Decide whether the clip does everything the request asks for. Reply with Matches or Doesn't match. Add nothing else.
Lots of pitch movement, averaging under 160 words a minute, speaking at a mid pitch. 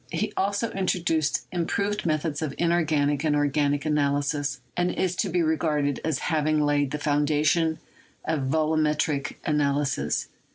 Doesn't match